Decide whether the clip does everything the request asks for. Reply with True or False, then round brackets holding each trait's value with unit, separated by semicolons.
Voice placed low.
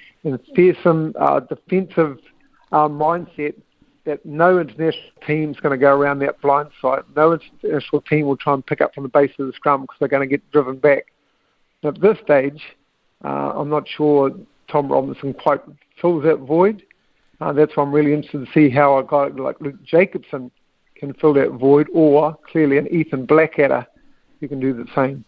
False (150 Hz)